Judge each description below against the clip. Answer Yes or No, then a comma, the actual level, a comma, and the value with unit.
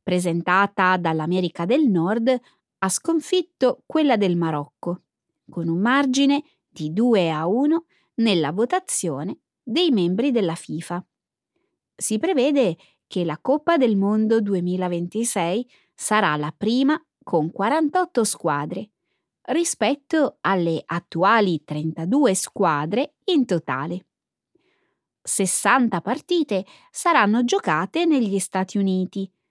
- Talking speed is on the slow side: Yes, slow, 100 wpm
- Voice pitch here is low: No, high, 205 Hz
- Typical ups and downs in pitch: No, wide, 7.5 semitones